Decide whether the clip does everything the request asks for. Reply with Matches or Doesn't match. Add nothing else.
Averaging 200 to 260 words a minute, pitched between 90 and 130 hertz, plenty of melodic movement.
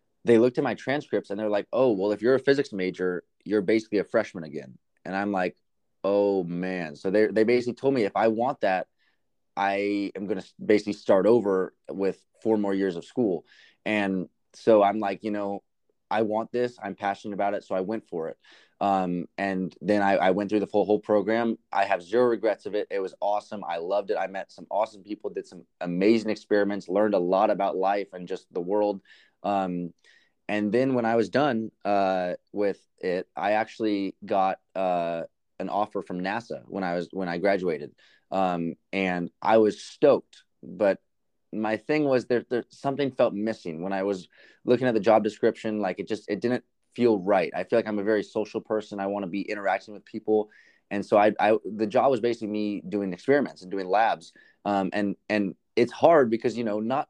Doesn't match